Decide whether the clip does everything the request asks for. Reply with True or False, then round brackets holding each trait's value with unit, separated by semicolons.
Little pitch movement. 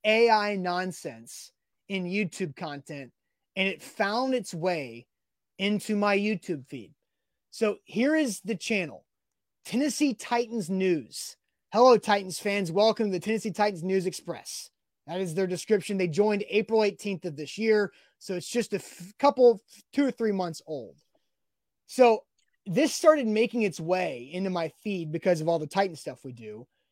False (3.8 semitones)